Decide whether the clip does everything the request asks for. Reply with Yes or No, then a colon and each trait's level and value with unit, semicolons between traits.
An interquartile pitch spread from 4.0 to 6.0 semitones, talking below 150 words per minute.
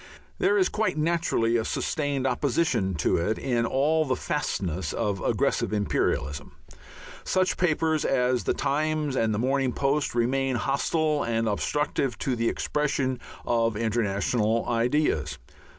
Yes: average, 4.6 semitones; slow, 135 wpm